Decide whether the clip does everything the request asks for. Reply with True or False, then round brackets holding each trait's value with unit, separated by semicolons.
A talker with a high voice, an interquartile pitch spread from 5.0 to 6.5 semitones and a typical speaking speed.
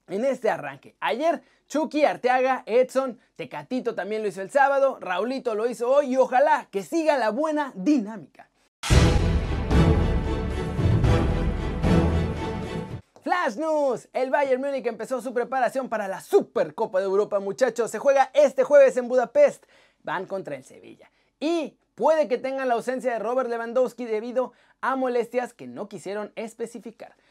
True (245 Hz; 5.5 semitones; 140 wpm)